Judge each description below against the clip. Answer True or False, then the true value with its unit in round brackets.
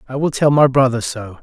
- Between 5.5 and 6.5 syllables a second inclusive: True (5.7 syllables/s)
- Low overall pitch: True (130 Hz)